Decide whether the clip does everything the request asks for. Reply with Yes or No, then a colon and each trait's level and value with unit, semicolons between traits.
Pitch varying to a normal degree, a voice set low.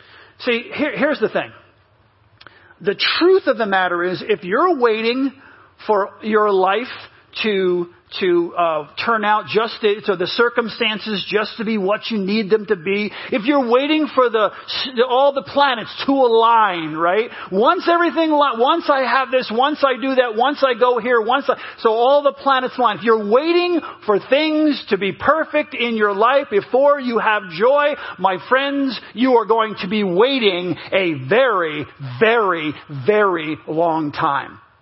No: average, 5.0 semitones; high, 225 Hz